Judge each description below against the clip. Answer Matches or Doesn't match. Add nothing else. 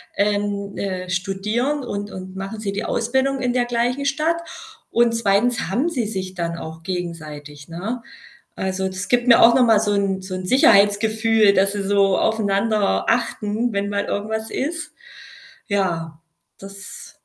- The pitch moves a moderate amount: Matches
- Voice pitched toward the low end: Doesn't match